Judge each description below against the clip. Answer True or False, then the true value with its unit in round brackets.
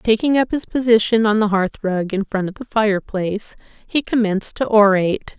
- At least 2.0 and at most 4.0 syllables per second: False (5.5 syllables/s)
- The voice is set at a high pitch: True (210 Hz)